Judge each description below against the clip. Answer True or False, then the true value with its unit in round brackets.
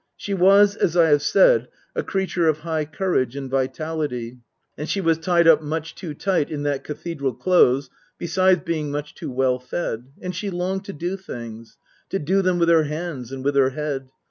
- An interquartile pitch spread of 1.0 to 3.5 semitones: False (4.7 semitones)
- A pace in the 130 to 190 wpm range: False (200 wpm)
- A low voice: False (155 Hz)